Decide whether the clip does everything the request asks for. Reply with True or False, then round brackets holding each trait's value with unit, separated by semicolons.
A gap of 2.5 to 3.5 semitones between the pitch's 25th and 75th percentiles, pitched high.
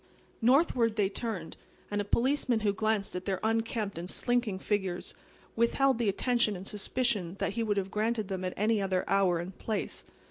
True (3.2 semitones; 210 Hz)